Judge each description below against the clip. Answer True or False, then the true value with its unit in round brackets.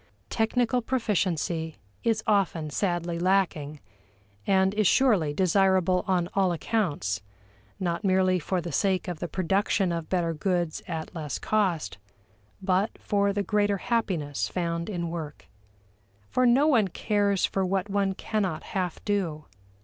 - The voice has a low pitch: False (185 Hz)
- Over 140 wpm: False (135 wpm)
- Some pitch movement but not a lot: True (3.3 semitones)